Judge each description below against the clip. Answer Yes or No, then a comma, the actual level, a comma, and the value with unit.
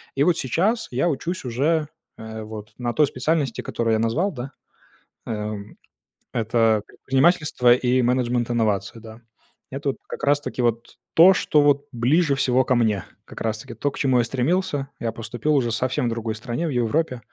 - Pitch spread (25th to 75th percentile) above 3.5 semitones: Yes, average, 4.0 semitones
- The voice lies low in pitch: Yes, low, 125 Hz